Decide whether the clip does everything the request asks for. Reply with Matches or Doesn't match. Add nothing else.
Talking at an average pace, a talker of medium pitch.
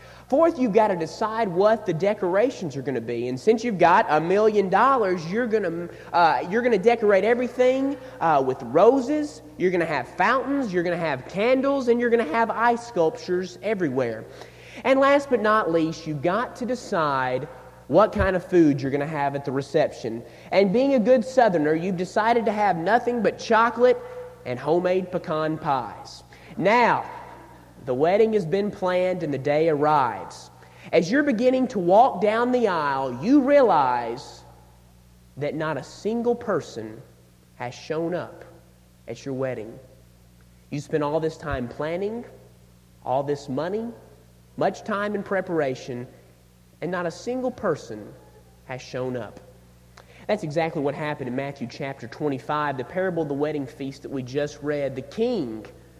Matches